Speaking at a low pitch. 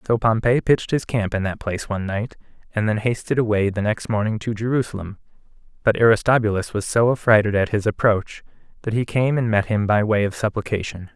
Yes: low, 110 Hz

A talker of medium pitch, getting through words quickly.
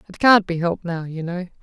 Yes: medium, 180 Hz; fast, 260 wpm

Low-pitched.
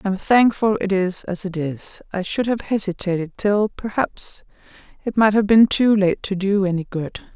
No: high, 200 Hz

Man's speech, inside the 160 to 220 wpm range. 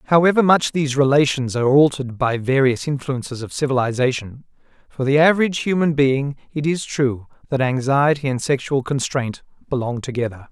No: male; average, 150 wpm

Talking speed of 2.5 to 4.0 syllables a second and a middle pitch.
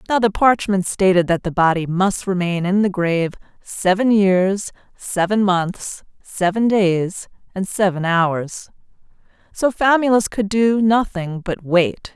No: 3.9 syllables/s; high, 195 Hz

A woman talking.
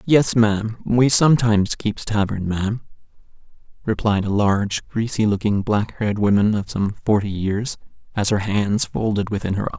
No: male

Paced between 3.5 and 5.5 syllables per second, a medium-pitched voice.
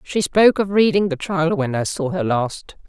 Yes: 4.8 syllables/s; medium, 170 Hz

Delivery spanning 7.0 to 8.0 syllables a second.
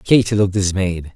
No: 5.4 syllables/s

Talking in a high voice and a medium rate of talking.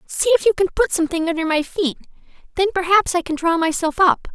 No: very high, 345 Hz; fast, 220 wpm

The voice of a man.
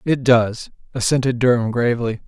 Yes: male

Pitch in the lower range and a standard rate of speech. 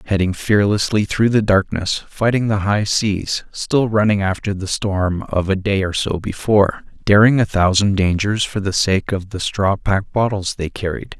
Yes: low, 100 Hz; average, 180 wpm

